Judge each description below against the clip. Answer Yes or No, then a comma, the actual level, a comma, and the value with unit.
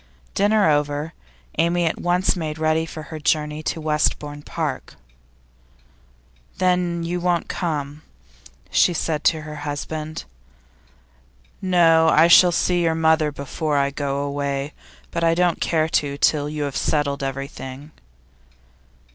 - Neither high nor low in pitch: Yes, medium, 155 Hz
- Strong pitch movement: No, narrow, 2.4 semitones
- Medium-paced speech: No, slow, 130 wpm